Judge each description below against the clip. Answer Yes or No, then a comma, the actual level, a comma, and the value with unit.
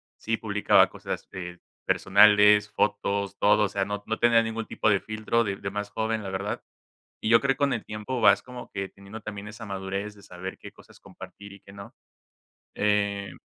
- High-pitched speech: No, low, 105 Hz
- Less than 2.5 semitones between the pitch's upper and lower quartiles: Yes, narrow, 1.8 semitones